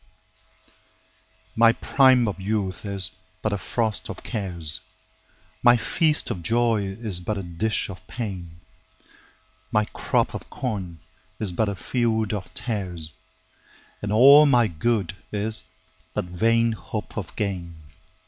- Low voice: Yes, low, 100 Hz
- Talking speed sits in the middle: No, slow, 120 wpm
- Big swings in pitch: No, average, 3.5 semitones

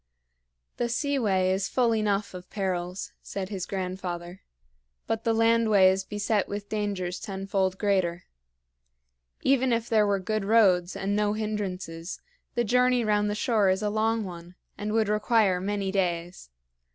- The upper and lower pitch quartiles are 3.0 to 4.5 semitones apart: No, narrow, 2.6 semitones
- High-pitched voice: Yes, high, 200 Hz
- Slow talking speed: No, average, 150 wpm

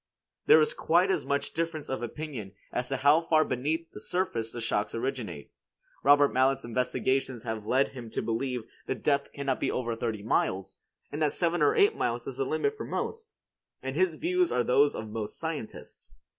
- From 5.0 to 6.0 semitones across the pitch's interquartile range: Yes, wide, 5.4 semitones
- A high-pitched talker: No, low, 135 Hz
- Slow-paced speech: No, average, 190 wpm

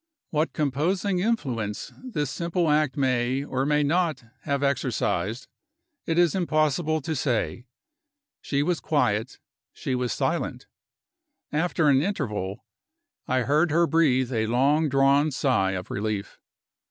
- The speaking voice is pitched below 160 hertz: Yes, medium, 140 Hz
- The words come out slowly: Yes, slow, 130 wpm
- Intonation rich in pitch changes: No, average, 4.1 semitones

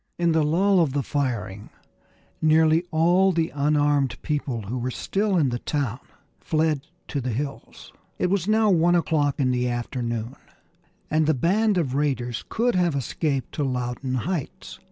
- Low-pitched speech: No, medium, 145 Hz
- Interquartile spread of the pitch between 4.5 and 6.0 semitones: Yes, average, 4.8 semitones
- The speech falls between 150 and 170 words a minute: Yes, average, 160 wpm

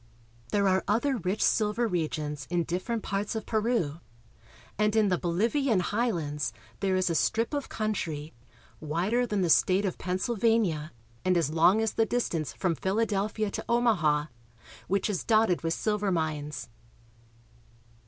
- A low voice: No, high, 195 Hz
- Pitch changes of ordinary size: Yes, average, 4.8 semitones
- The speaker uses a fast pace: No, average, 145 wpm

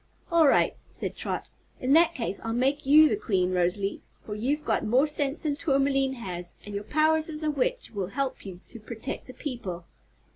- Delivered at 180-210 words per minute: Yes, average, 195 wpm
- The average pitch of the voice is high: Yes, very high, 265 Hz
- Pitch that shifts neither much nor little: No, wide, 6.5 semitones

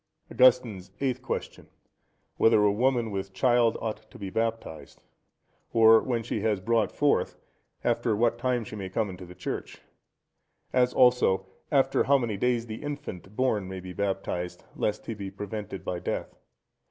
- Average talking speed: Yes, average, 155 wpm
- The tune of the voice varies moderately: Yes, average, 4.1 semitones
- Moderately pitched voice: No, low, 110 Hz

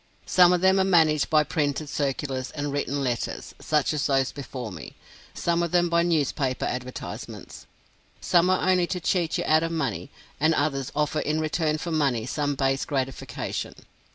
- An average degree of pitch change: Yes, average, 3.7 semitones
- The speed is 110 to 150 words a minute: No, average, 175 wpm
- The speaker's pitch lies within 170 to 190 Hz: No, medium, 150 Hz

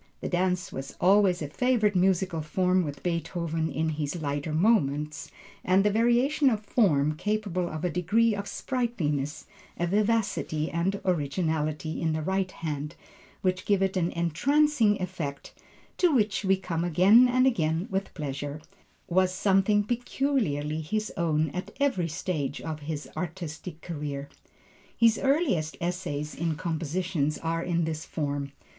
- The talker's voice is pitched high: No, medium, 175 Hz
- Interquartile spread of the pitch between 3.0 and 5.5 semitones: Yes, average, 4.7 semitones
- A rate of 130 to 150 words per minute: Yes, average, 140 wpm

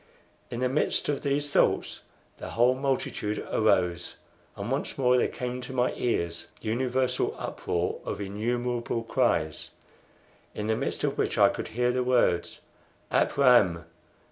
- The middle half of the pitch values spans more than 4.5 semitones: No, average, 3.4 semitones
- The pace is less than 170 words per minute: Yes, average, 150 wpm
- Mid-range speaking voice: No, low, 125 Hz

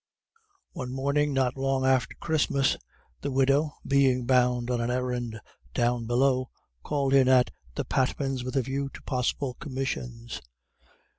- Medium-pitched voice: No, low, 130 Hz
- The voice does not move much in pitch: Yes, narrow, 1.7 semitones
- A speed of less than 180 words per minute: Yes, average, 140 wpm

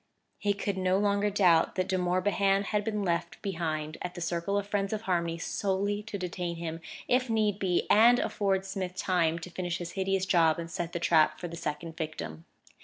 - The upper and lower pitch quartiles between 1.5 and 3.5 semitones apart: Yes, average, 3.0 semitones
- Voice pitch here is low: No, medium, 185 Hz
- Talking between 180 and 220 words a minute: Yes, average, 200 wpm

